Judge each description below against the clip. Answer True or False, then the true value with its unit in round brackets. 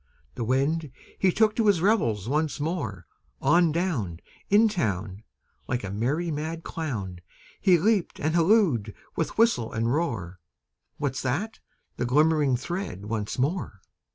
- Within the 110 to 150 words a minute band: True (140 wpm)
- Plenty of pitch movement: True (7.6 semitones)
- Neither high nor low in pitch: True (150 Hz)